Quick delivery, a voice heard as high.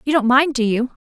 Yes: fast, 290 wpm; very high, 255 Hz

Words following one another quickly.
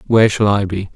Yes: fast, 255 wpm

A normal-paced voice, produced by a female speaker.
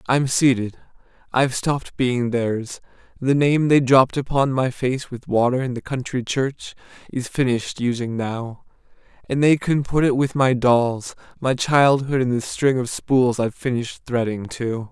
No: average, 170 wpm; male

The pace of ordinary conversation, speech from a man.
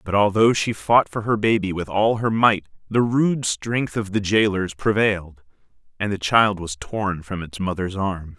Yes: average, 195 wpm; male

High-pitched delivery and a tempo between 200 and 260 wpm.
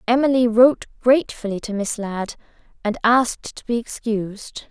No: high, 230 Hz; average, 140 wpm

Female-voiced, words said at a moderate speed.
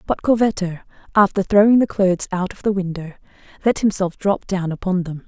Yes: female; average, 180 wpm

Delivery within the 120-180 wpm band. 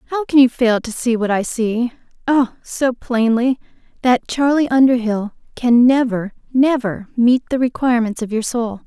Yes: average, 160 wpm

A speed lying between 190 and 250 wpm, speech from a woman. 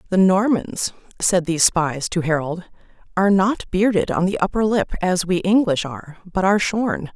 No: average, 175 wpm; female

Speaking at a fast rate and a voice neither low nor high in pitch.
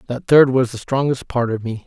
No: fast, 255 wpm; low, 125 Hz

